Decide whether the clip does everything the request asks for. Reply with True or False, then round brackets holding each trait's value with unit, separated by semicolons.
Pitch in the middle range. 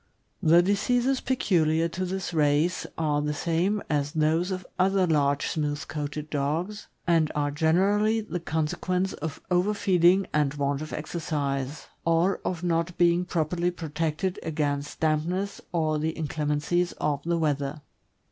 True (165 Hz)